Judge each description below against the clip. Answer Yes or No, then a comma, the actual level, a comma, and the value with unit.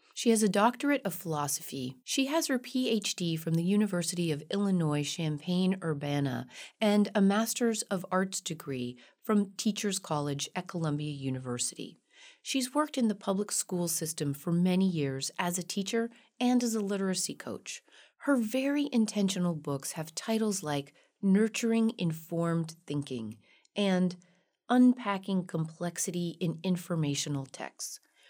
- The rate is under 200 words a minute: Yes, slow, 135 wpm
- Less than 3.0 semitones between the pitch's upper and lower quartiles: No, wide, 5.5 semitones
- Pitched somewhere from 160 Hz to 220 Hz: Yes, medium, 185 Hz